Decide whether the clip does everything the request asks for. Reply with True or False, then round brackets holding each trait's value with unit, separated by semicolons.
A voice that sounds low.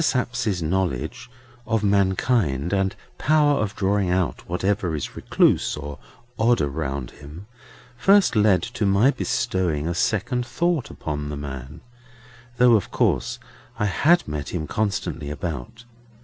True (95 Hz)